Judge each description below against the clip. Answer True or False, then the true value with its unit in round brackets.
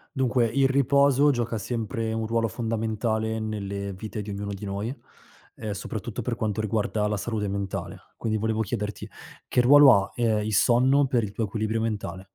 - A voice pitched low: True (110 Hz)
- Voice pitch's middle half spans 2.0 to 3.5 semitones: True (2.4 semitones)